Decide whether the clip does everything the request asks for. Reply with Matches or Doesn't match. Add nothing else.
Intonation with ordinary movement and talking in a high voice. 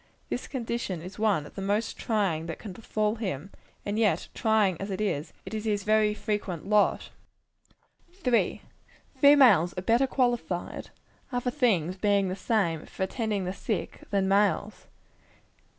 Matches